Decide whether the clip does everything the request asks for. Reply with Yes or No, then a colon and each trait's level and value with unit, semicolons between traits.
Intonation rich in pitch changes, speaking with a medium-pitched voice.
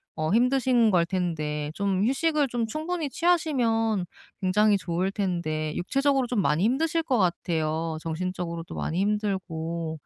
No: wide, 6.7 semitones; high, 195 Hz